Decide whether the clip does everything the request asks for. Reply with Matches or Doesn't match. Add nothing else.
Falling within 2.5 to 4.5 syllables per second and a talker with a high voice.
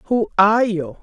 Matches